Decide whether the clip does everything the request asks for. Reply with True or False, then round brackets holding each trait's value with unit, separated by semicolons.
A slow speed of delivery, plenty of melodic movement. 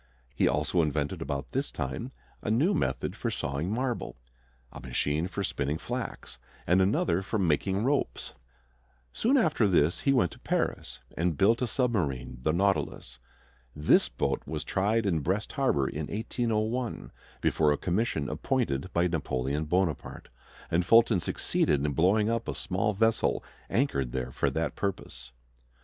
False (150 wpm; 7.3 semitones)